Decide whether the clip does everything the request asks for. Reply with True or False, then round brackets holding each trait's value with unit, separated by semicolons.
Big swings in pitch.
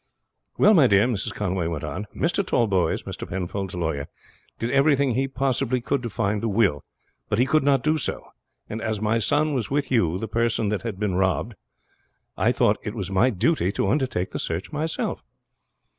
True (5.9 semitones)